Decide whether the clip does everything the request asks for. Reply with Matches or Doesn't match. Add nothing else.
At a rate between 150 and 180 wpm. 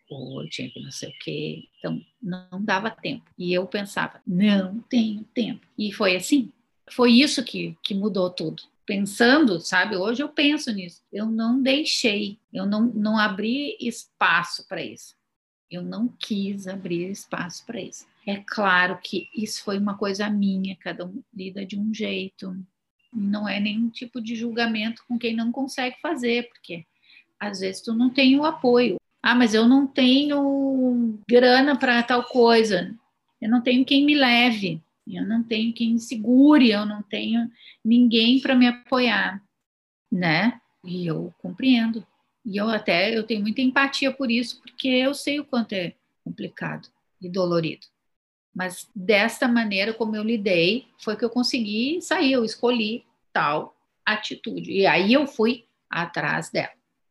Matches